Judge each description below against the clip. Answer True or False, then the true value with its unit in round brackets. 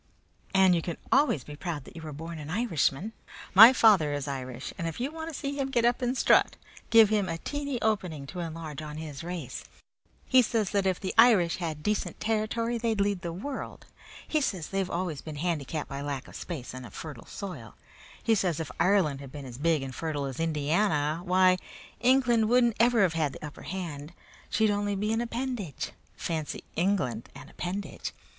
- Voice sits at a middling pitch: True (180 Hz)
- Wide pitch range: True (6.5 semitones)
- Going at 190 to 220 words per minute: True (200 wpm)